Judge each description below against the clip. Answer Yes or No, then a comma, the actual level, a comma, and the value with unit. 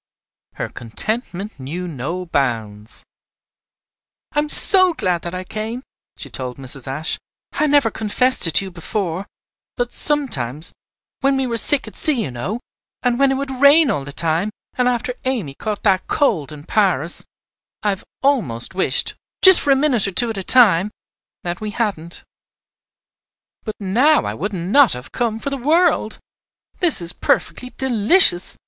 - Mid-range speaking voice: No, high, 210 Hz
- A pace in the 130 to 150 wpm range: No, average, 165 wpm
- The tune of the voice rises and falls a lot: Yes, wide, 7.6 semitones